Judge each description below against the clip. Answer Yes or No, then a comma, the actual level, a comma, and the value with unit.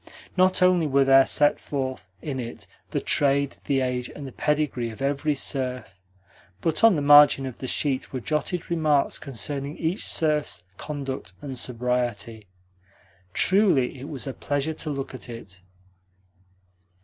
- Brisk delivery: No, average, 150 wpm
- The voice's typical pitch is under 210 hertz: Yes, medium, 140 Hz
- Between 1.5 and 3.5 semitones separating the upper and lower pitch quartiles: Yes, average, 2.9 semitones